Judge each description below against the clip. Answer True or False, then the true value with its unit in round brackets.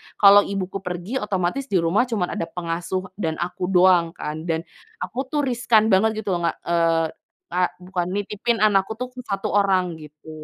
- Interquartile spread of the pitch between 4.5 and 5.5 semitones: False (3.8 semitones)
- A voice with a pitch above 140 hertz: True (190 Hz)